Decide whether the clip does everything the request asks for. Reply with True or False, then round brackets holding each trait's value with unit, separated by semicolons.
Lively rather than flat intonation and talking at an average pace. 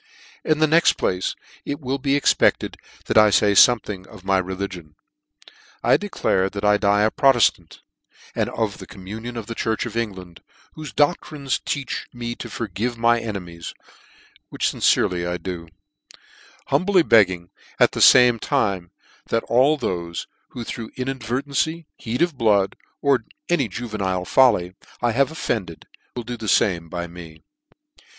True (5.7 semitones; 155 wpm)